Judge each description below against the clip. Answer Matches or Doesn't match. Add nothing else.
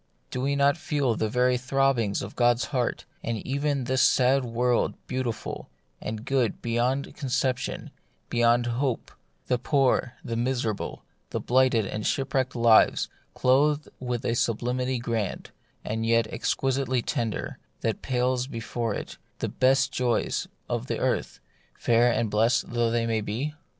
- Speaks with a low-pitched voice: Matches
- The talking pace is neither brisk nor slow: Matches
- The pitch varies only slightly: Matches